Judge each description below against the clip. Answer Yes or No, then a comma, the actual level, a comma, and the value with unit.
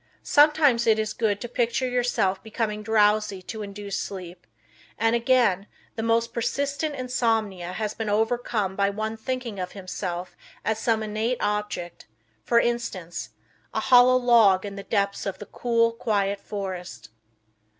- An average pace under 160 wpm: Yes, average, 145 wpm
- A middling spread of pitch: Yes, average, 3.0 semitones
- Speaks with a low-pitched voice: No, high, 215 Hz